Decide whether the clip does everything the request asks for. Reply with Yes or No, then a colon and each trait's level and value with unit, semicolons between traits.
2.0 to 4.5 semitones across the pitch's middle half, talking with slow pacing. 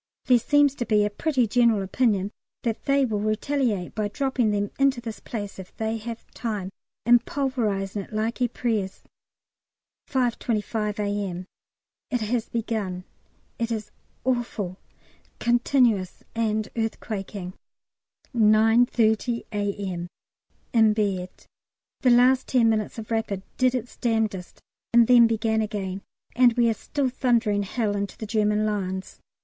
Yes: average, 2.8 semitones; slow, 130 wpm